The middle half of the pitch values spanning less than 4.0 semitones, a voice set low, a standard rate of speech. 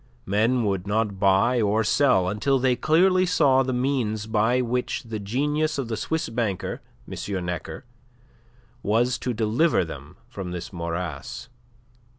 No: average, 4.8 semitones; low, 110 Hz; average, 145 wpm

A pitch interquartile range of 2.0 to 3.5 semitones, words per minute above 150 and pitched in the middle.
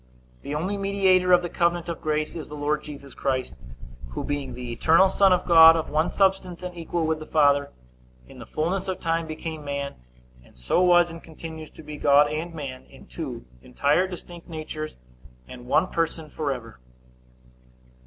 Yes: average, 3.1 semitones; average, 180 wpm; medium, 160 Hz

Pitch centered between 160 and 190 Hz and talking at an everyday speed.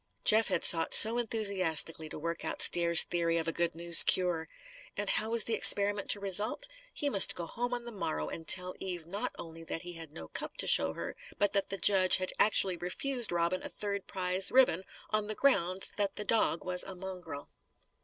No: medium, 185 Hz; fast, 210 wpm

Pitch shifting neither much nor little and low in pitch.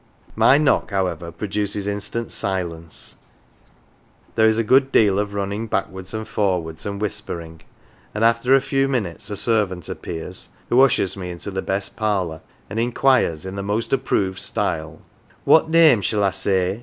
Yes: average, 3.5 semitones; low, 100 Hz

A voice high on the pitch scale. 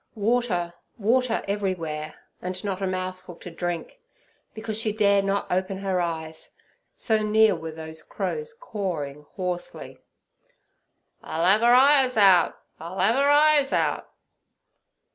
Yes: high, 195 Hz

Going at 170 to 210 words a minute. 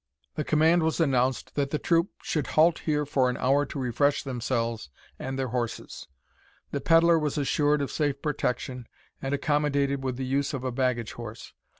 Yes: average, 180 wpm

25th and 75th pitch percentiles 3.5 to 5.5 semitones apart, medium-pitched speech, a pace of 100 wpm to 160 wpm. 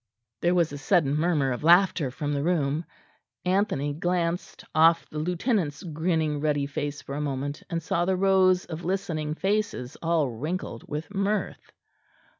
Yes: average, 3.8 semitones; medium, 165 Hz; average, 155 wpm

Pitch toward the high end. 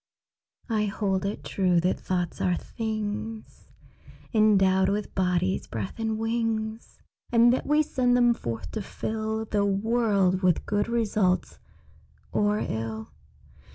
Yes: high, 210 Hz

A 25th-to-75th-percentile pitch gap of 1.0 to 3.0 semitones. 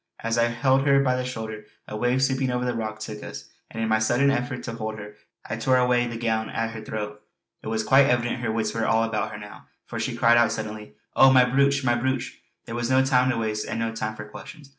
Yes: narrow, 2.6 semitones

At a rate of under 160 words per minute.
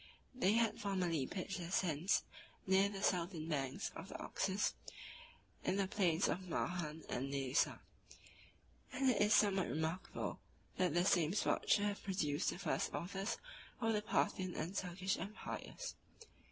Yes: average, 150 wpm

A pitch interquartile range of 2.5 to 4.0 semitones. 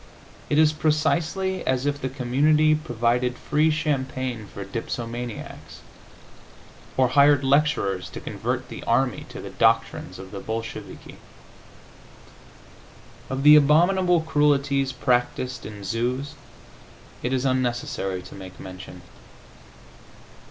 No: average, 4.6 semitones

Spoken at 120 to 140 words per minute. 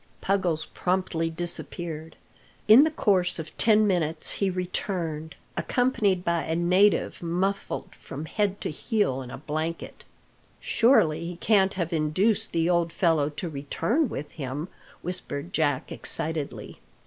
Yes: slow, 135 wpm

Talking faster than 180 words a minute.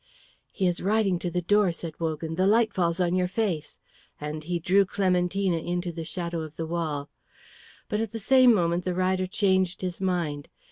Yes: average, 190 wpm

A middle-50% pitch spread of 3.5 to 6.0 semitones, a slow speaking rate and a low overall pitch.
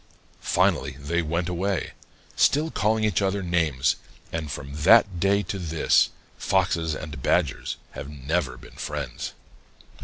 Yes: average, 4.4 semitones; slow, 130 wpm; very low, 85 Hz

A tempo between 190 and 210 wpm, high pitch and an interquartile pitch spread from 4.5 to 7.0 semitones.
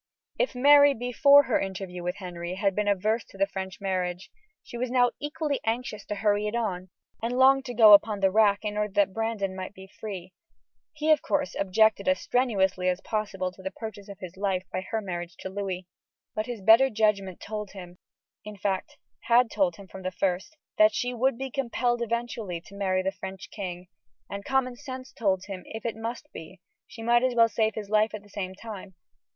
No: fast, 205 wpm; high, 210 Hz; average, 3.8 semitones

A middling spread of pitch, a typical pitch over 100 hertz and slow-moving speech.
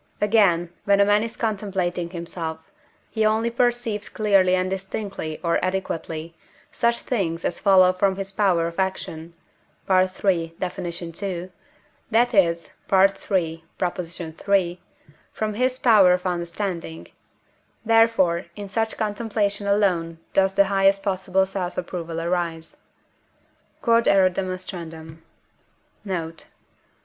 Yes: average, 3.1 semitones; high, 190 Hz; slow, 110 wpm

